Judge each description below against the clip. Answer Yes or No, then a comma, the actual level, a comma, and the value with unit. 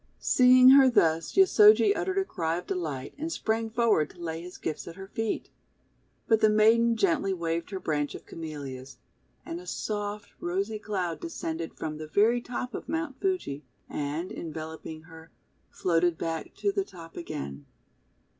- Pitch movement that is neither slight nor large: No, wide, 6.2 semitones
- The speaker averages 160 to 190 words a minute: Yes, average, 165 wpm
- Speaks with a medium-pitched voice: Yes, medium, 180 Hz